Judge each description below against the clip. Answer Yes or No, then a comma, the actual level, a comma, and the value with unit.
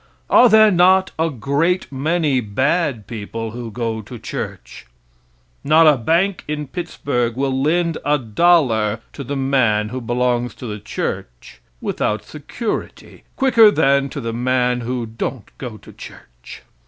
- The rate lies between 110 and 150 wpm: Yes, average, 145 wpm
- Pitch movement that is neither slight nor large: No, wide, 5.8 semitones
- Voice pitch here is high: No, low, 130 Hz